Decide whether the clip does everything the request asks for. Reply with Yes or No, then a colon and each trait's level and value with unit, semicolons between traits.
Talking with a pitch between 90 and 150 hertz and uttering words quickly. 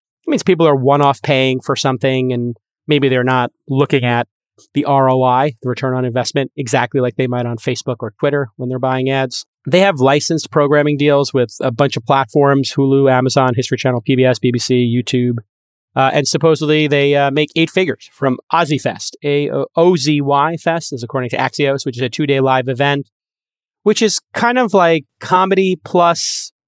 No: low, 135 Hz; average, 185 wpm